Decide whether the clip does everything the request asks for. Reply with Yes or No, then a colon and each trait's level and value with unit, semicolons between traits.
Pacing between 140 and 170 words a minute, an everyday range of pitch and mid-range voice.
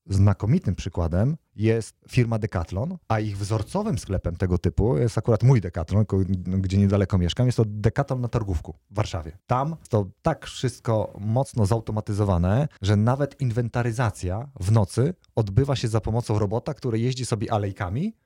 No: average, 150 wpm; average, 3.7 semitones; low, 110 Hz